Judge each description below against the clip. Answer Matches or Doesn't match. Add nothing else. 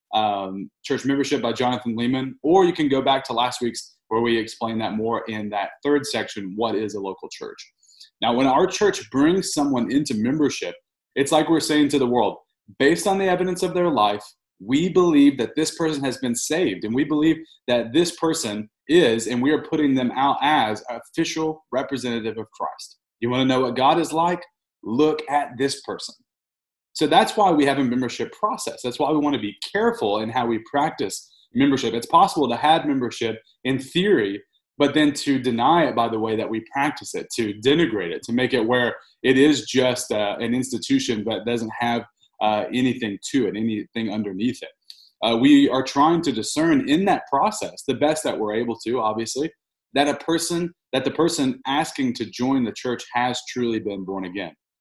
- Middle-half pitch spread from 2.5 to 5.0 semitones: Doesn't match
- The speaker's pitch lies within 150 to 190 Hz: Doesn't match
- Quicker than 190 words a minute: Matches